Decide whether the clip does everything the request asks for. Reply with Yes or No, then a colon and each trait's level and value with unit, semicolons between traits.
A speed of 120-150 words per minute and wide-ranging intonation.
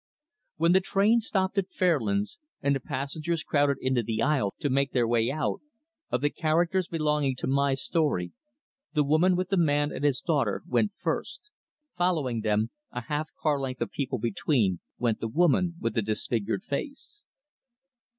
No: average, 170 wpm; wide, 5.8 semitones